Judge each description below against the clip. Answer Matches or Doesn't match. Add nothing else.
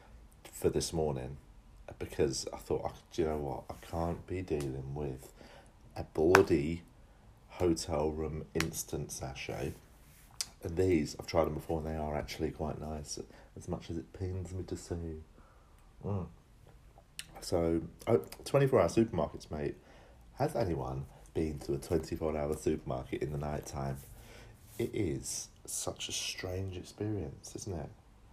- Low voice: Matches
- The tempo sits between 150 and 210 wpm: Doesn't match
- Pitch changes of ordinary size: Matches